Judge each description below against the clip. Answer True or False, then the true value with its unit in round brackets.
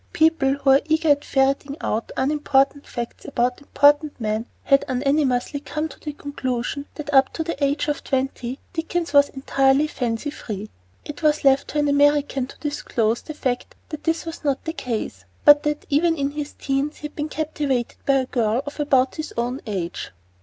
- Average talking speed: True (190 wpm)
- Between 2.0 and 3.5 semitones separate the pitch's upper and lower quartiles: True (2.4 semitones)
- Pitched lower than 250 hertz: False (280 Hz)